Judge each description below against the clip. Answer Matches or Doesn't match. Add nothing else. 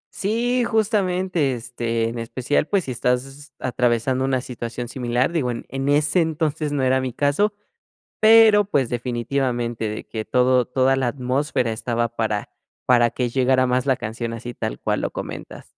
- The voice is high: Doesn't match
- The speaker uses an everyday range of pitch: Matches